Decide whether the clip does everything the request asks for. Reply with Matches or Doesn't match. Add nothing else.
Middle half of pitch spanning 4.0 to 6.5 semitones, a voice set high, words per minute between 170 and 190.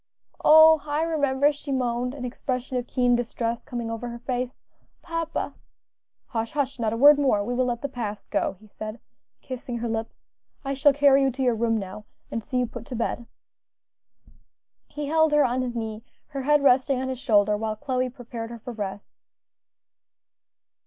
Doesn't match